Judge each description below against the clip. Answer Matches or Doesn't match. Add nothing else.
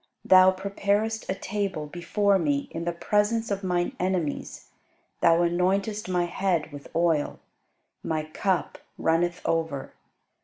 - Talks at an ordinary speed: Doesn't match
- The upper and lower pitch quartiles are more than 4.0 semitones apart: Doesn't match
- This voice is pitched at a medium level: Matches